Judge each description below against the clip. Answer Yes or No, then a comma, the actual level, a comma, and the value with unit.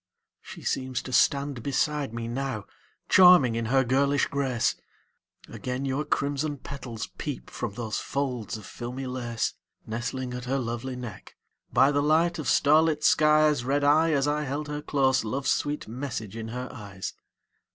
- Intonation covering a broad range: No, average, 3.3 semitones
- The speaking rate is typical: Yes, average, 160 wpm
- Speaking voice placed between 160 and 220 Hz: No, low, 135 Hz